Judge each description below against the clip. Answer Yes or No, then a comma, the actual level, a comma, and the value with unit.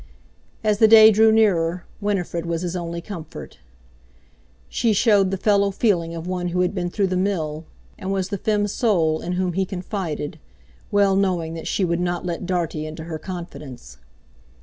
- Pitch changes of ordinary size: Yes, average, 3.1 semitones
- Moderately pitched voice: Yes, medium, 180 Hz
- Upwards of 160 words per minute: Yes, average, 175 wpm